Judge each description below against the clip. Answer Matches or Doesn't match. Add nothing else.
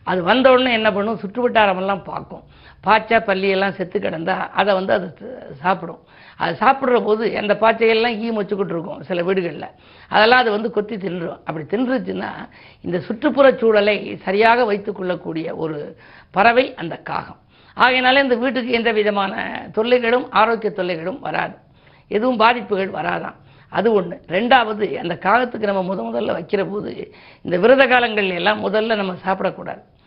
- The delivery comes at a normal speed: Doesn't match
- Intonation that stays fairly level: Doesn't match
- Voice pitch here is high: Matches